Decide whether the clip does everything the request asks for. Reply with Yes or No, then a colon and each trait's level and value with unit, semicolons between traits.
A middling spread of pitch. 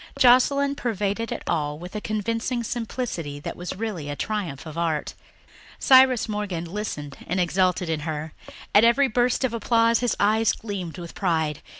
No: wide, 5.9 semitones